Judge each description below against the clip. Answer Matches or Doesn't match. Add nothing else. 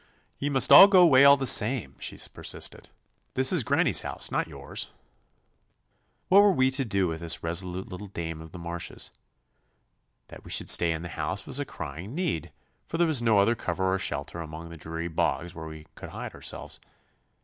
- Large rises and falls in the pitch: Matches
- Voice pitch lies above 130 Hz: Doesn't match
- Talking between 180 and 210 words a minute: Matches